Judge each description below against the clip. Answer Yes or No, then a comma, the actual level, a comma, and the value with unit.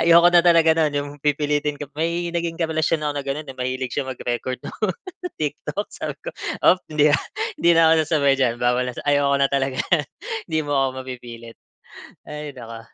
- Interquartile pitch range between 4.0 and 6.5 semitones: No, average, 3.5 semitones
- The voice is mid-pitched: Yes, medium, 145 Hz